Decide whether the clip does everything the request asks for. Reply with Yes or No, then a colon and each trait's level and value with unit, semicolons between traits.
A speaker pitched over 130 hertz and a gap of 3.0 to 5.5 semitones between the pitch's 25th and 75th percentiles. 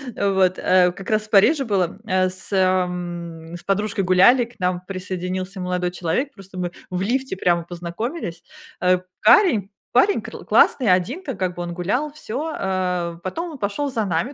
Yes: medium, 185 Hz; average, 3.9 semitones